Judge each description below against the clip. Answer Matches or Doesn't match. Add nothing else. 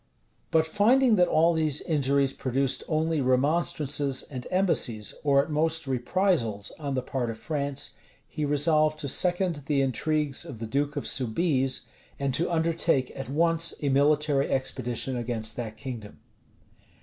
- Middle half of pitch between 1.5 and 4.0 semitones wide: Matches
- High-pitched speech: Doesn't match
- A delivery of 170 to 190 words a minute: Doesn't match